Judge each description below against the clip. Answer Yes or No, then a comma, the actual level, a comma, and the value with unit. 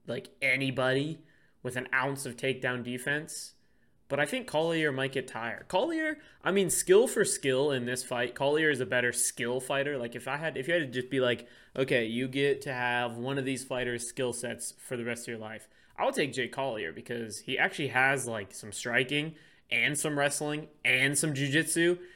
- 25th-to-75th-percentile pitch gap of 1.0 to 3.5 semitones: Yes, average, 3.1 semitones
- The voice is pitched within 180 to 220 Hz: No, low, 130 Hz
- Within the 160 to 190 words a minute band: No, fast, 205 wpm